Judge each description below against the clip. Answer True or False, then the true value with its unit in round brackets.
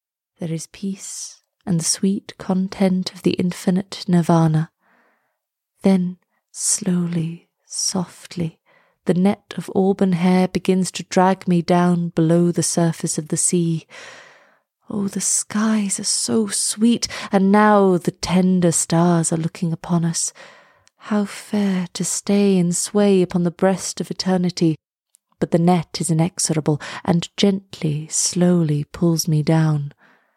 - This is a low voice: False (180 Hz)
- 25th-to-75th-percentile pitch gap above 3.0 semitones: False (2.5 semitones)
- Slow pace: True (130 wpm)